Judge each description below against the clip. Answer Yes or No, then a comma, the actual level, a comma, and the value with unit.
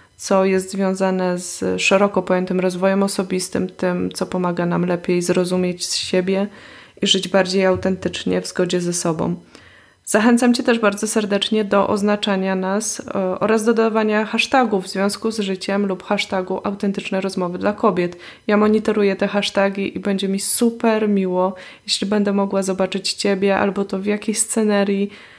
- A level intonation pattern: Yes, narrow, 1.9 semitones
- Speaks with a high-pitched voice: Yes, high, 195 Hz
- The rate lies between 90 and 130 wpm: No, average, 155 wpm